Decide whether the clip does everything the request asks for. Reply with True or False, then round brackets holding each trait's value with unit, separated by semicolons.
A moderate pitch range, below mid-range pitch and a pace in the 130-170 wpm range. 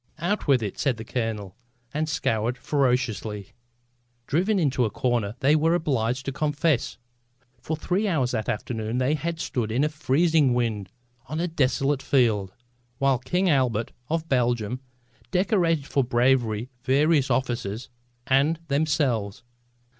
True (4.9 semitones; 130 Hz; 140 wpm)